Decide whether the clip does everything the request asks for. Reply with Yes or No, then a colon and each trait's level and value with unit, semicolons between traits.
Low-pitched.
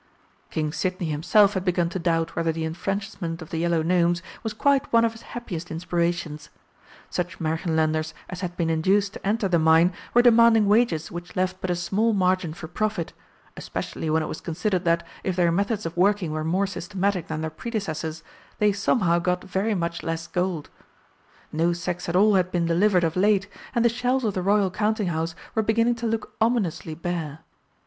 No: medium, 180 Hz